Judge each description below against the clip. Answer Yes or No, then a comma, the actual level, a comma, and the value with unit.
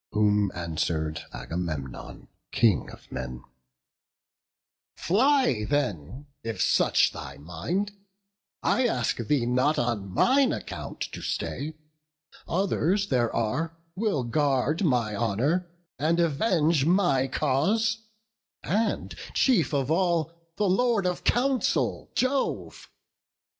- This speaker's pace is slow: Yes, slow, 105 wpm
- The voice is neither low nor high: Yes, medium, 145 Hz